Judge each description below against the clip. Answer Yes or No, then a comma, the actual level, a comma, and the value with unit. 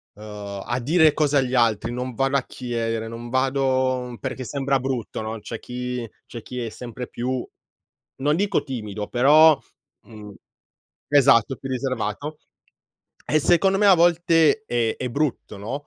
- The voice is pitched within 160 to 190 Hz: No, low, 130 Hz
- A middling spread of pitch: Yes, average, 3.5 semitones